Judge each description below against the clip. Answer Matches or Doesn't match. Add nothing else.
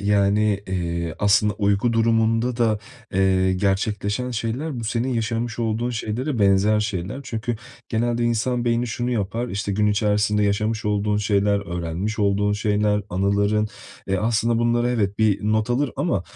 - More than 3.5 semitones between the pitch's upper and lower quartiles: Doesn't match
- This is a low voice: Matches